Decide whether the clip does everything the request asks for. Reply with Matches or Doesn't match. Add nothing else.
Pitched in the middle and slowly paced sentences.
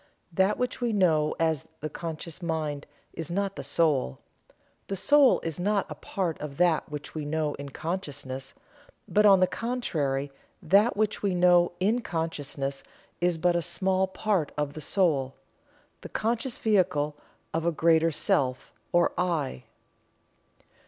Doesn't match